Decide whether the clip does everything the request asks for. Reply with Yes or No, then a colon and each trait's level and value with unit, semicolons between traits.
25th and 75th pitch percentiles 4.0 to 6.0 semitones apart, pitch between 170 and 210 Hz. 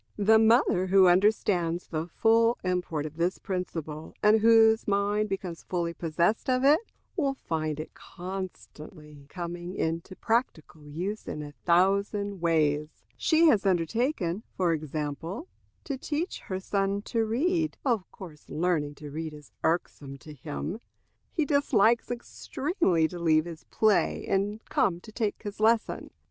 Yes: average, 5.3 semitones; medium, 185 Hz